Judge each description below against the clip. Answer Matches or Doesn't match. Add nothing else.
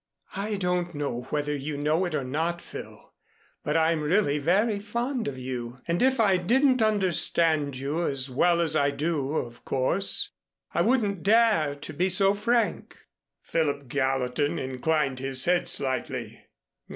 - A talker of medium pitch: Matches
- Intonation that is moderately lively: Doesn't match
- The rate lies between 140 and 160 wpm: Matches